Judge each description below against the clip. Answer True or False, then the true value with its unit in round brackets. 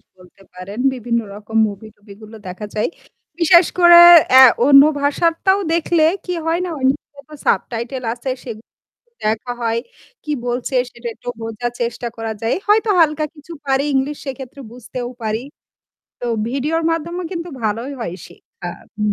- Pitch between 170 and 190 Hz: False (250 Hz)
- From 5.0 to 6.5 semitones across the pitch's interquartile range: True (5.4 semitones)